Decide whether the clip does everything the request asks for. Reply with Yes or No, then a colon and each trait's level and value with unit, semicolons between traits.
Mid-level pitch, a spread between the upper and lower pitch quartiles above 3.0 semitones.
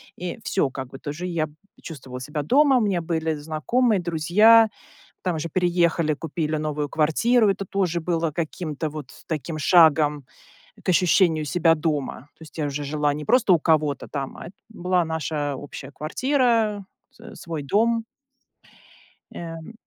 Yes: medium, 160 Hz; average, 3.5 semitones